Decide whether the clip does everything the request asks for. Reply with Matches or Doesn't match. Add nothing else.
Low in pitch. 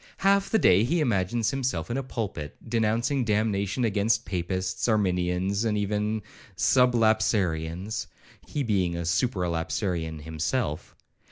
Matches